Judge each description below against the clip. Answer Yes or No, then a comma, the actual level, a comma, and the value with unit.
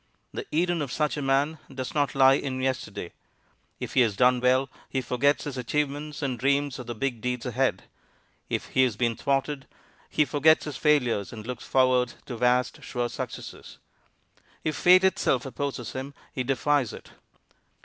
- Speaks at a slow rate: No, average, 170 wpm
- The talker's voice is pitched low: Yes, low, 130 Hz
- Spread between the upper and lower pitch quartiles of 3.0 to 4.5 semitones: No, narrow, 2.6 semitones